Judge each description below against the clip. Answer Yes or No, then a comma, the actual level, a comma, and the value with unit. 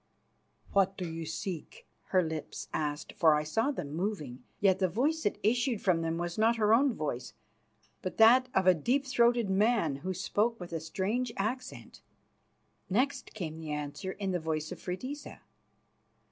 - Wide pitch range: Yes, wide, 6.1 semitones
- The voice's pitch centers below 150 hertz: No, high, 190 Hz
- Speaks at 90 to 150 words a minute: No, average, 170 wpm